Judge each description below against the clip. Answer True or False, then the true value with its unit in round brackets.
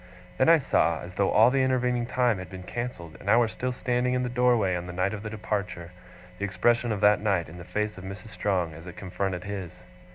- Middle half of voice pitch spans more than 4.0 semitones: True (4.8 semitones)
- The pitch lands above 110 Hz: False (105 Hz)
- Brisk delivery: True (240 wpm)